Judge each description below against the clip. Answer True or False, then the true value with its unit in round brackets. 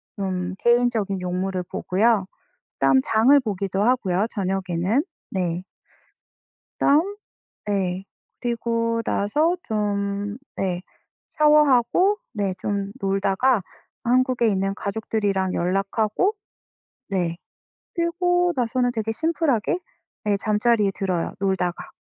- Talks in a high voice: True (205 Hz)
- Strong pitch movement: False (4.2 semitones)